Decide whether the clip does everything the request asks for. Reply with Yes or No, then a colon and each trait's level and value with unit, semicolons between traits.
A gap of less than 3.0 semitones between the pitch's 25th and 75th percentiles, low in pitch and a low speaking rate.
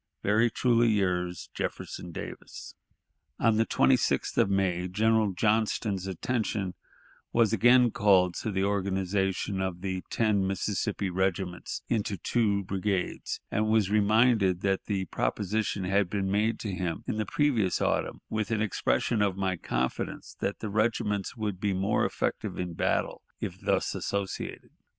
No: narrow, 2.5 semitones; low, 100 Hz; average, 145 wpm